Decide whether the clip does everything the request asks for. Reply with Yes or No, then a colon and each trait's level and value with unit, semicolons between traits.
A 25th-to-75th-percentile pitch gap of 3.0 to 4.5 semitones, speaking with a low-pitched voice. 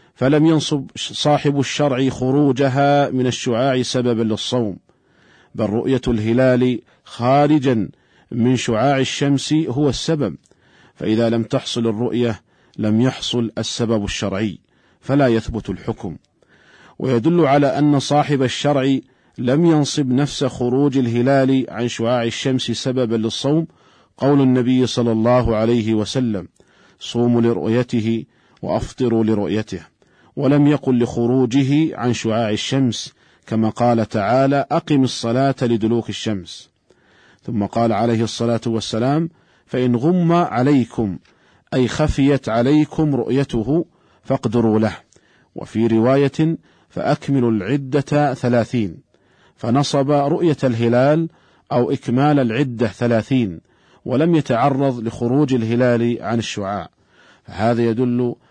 Yes: average, 3.4 semitones; low, 125 Hz